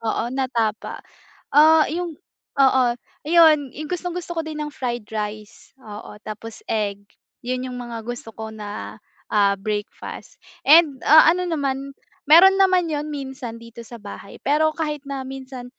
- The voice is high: Yes, very high, 265 Hz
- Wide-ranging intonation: Yes, wide, 5.7 semitones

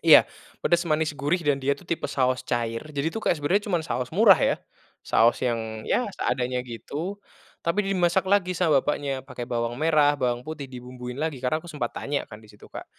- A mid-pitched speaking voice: Yes, medium, 145 Hz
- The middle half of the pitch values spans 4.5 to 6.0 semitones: Yes, average, 5.2 semitones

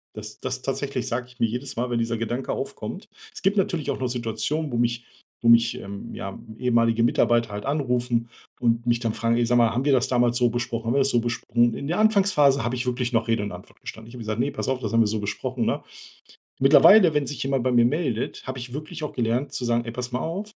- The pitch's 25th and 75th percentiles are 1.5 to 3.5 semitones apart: Yes, narrow, 2.6 semitones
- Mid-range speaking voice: No, low, 120 Hz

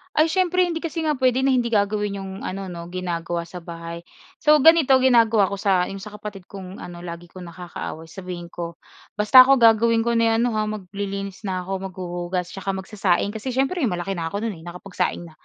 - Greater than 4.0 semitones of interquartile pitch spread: Yes, average, 4.7 semitones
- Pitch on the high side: Yes, high, 195 Hz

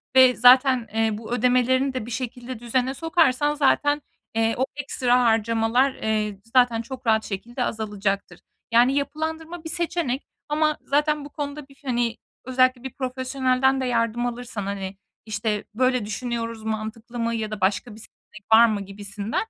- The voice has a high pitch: Yes, high, 245 Hz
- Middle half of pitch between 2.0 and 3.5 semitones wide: Yes, average, 3.1 semitones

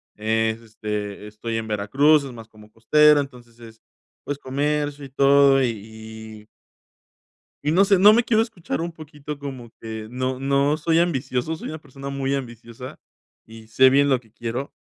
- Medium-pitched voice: No, low, 130 Hz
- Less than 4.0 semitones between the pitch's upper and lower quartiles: No, average, 4.5 semitones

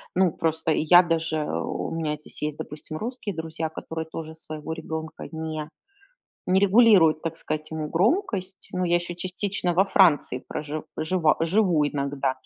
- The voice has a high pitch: No, medium, 160 Hz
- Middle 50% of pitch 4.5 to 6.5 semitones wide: No, average, 2.9 semitones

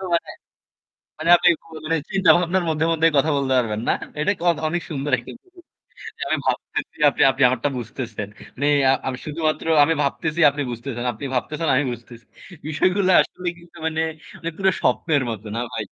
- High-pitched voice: No, medium, 145 Hz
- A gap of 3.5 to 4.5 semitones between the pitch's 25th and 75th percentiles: No, average, 5.3 semitones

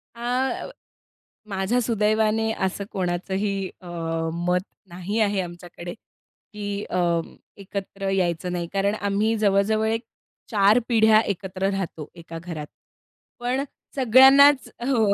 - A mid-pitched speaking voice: No, high, 200 Hz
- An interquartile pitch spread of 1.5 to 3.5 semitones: Yes, average, 3.2 semitones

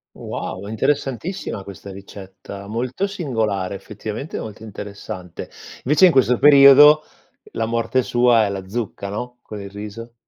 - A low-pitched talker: Yes, low, 110 Hz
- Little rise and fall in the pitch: No, average, 4.6 semitones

